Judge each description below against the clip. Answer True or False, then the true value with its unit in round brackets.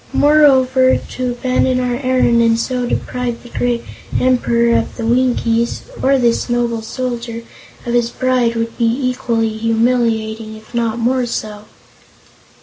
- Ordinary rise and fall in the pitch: False (1.6 semitones)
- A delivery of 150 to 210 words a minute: False (140 wpm)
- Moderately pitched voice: False (240 Hz)